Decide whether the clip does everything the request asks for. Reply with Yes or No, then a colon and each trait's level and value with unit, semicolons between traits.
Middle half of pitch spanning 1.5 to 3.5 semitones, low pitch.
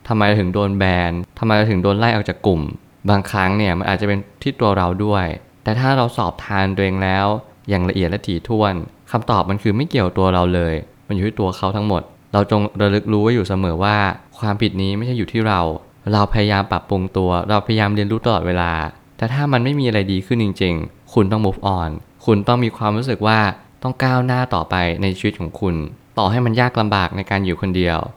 Yes: average, 2.9 semitones; low, 100 Hz